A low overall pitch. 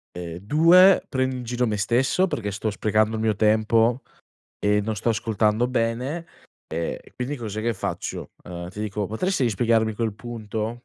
Yes: low, 110 Hz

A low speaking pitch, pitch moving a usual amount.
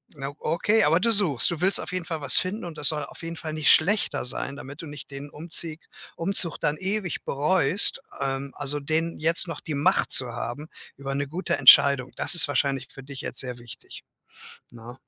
No: medium, 150 Hz; average, 3.5 semitones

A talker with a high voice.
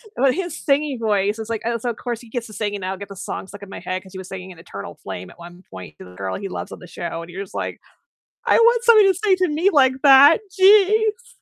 Yes: high, 220 Hz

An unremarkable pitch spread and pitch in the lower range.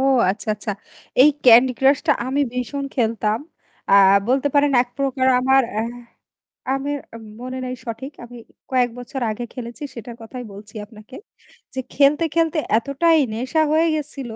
No: average, 3.2 semitones; very high, 260 Hz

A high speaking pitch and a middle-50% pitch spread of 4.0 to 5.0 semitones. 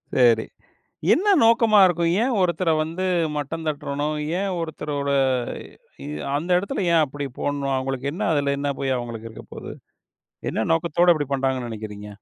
No: medium, 145 Hz; average, 4.4 semitones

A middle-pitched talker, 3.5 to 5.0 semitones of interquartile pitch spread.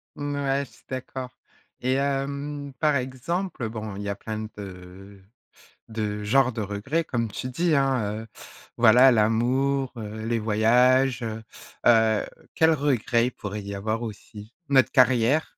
No: low, 120 Hz; average, 4.0 semitones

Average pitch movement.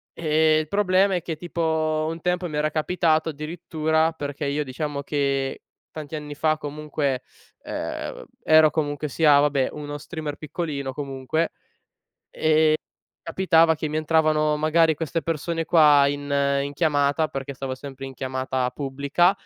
No: narrow, 2.2 semitones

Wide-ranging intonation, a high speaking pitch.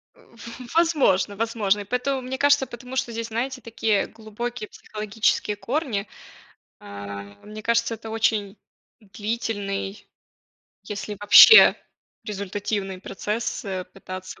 No: average, 2.8 semitones; high, 215 Hz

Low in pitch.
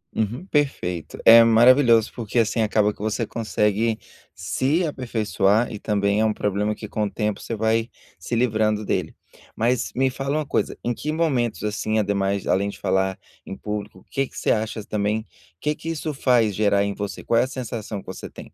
Yes: low, 110 Hz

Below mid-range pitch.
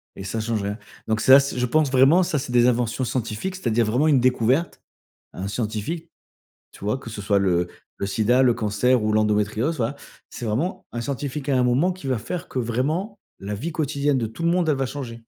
Yes: low, 125 Hz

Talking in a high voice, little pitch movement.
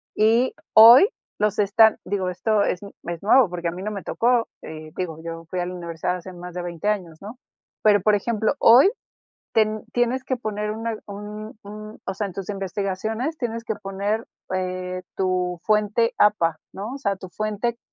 No: high, 205 Hz; average, 3.2 semitones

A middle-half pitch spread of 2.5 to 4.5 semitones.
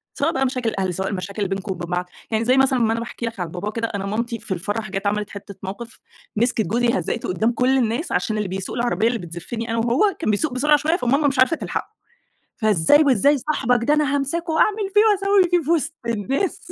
No: wide, 5.6 semitones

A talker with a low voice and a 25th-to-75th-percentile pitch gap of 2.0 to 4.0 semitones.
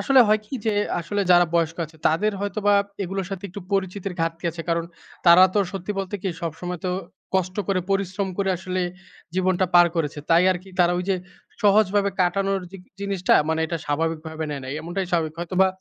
No: medium, 185 Hz; average, 2.8 semitones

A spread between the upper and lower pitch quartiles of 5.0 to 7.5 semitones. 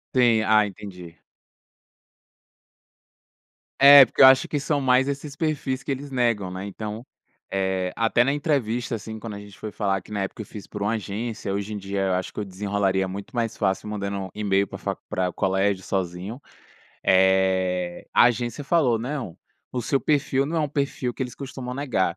Yes: average, 5.3 semitones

